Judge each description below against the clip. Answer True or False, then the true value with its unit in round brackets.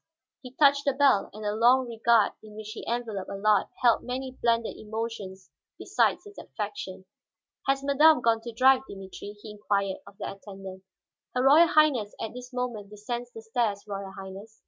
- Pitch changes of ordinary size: True (3.7 semitones)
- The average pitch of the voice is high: True (225 Hz)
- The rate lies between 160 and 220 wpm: True (170 wpm)